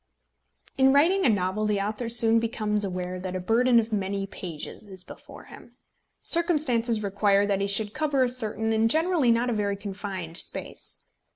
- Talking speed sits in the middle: Yes, average, 175 wpm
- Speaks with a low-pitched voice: No, high, 215 Hz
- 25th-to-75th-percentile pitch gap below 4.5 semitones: Yes, average, 3.5 semitones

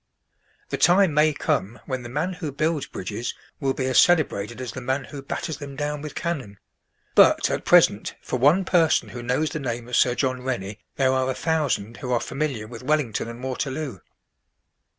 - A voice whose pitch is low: Yes, low, 130 Hz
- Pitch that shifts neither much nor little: Yes, average, 3.9 semitones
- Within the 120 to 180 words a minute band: No, average, 190 wpm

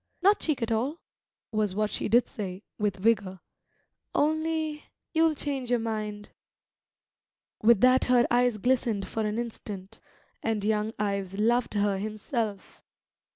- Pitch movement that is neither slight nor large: Yes, average, 3.3 semitones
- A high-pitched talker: Yes, high, 220 Hz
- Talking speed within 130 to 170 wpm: Yes, slow, 135 wpm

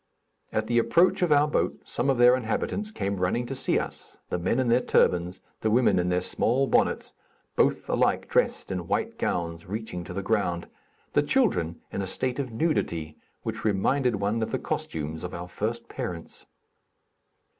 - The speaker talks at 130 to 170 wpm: No, average, 180 wpm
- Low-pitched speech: Yes, low, 110 Hz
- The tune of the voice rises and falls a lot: Yes, wide, 6.1 semitones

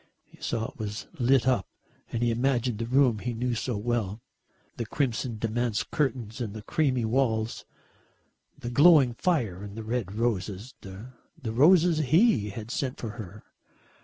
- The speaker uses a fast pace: No, average, 160 wpm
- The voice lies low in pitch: Yes, low, 120 Hz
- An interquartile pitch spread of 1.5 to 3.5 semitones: Yes, average, 3.1 semitones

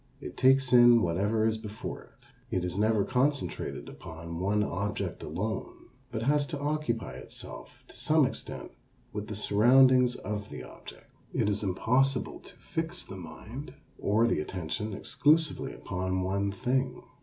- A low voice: Yes, low, 110 Hz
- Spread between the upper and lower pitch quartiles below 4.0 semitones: No, average, 4.8 semitones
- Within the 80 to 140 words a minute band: No, average, 150 wpm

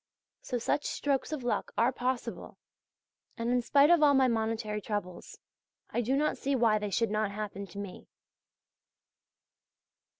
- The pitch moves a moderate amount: Yes, average, 4.0 semitones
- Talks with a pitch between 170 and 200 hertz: No, high, 235 Hz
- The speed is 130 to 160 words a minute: Yes, average, 155 wpm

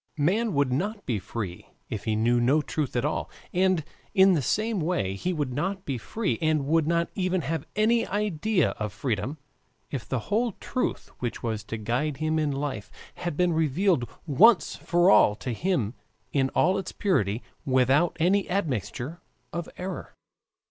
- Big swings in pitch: Yes, wide, 6.8 semitones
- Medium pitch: Yes, medium, 155 Hz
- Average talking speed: Yes, average, 170 wpm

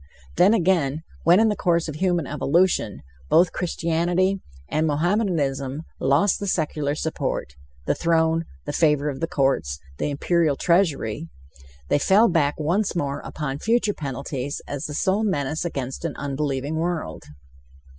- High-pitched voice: No, medium, 160 Hz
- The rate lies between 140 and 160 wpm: Yes, average, 145 wpm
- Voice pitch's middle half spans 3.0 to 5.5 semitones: Yes, average, 3.9 semitones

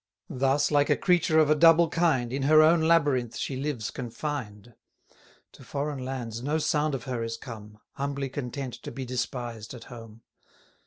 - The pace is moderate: Yes, average, 170 wpm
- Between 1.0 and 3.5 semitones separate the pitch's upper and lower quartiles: No, average, 3.9 semitones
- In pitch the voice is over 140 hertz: No, low, 135 Hz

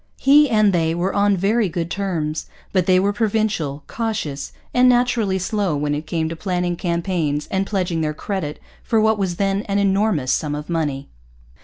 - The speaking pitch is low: No, medium, 185 Hz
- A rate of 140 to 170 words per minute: No, average, 180 wpm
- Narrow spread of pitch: No, average, 4.2 semitones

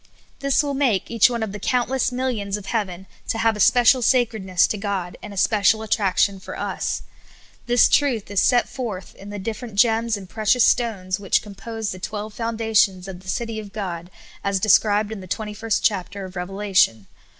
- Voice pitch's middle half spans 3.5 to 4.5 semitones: No, average, 2.9 semitones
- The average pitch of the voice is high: Yes, high, 210 Hz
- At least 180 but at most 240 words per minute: Yes, average, 195 wpm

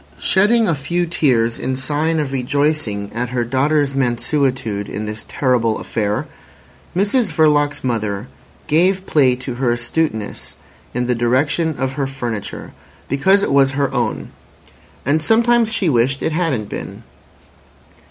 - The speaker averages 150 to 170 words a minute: No, average, 140 wpm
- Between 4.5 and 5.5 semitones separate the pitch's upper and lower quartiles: Yes, average, 4.8 semitones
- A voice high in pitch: No, low, 135 Hz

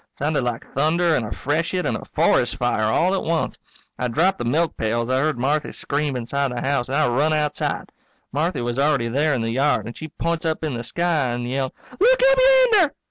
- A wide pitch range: No, average, 4.7 semitones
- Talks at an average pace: No, fast, 220 wpm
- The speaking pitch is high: No, medium, 140 Hz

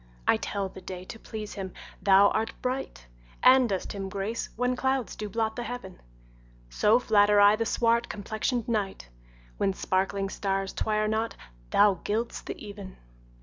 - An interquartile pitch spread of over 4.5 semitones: No, average, 2.8 semitones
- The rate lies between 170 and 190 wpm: No, average, 160 wpm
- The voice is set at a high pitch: Yes, high, 210 Hz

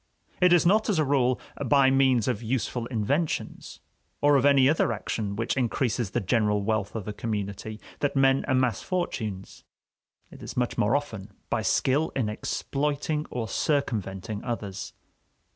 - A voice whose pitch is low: Yes, low, 125 Hz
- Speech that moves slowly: No, average, 155 wpm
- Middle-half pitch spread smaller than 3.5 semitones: No, average, 4.8 semitones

